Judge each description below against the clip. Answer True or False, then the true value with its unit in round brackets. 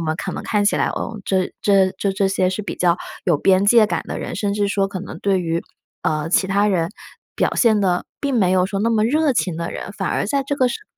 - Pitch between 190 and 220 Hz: True (195 Hz)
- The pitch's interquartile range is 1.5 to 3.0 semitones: True (2.7 semitones)